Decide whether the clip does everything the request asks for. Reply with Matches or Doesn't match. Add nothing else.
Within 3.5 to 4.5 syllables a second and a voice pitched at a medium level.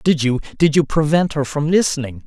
Doesn't match